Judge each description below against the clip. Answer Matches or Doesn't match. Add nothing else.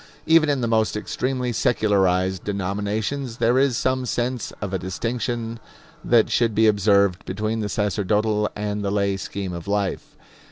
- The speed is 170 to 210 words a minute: Doesn't match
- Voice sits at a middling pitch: Doesn't match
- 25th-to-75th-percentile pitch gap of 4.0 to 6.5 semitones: Doesn't match